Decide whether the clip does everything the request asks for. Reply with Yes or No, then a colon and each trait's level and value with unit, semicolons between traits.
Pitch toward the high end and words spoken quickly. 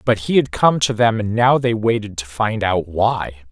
No: low, 110 Hz; fast, 240 wpm